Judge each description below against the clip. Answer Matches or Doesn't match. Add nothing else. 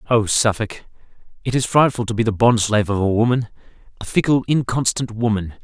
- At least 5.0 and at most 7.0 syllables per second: Matches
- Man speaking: Matches